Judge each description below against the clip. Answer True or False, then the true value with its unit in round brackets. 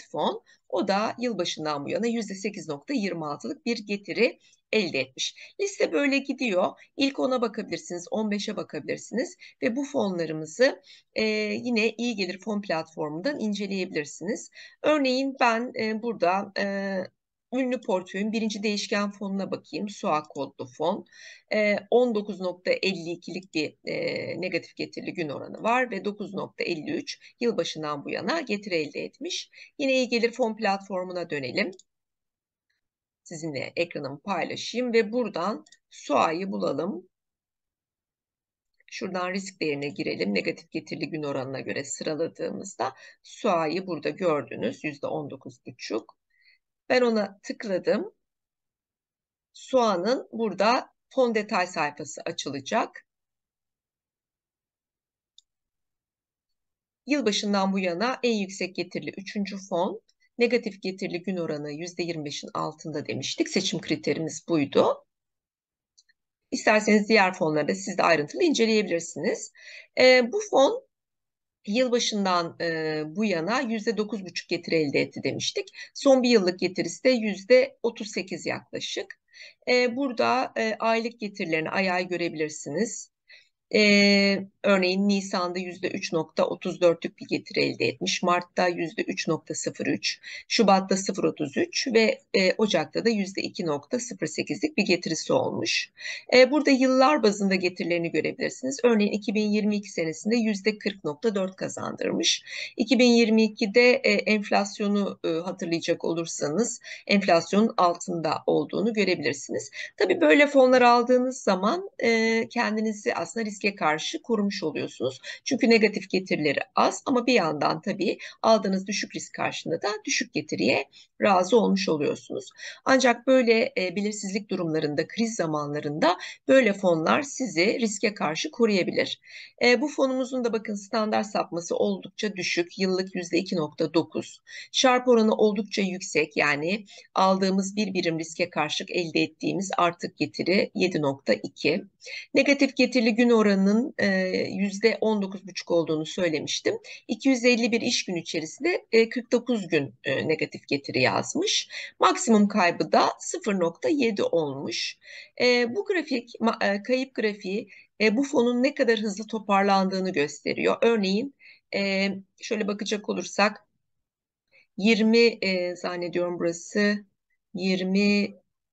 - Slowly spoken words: False (110 wpm)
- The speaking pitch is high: True (210 Hz)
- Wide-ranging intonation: True (5.7 semitones)